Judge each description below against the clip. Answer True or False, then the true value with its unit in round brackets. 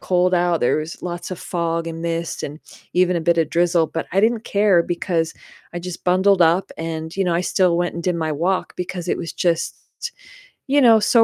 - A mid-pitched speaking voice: True (175 Hz)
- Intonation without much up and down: True (1.8 semitones)